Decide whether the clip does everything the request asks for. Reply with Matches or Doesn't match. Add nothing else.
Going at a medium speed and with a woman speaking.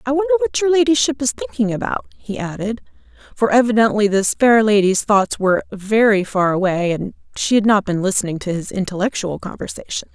Matches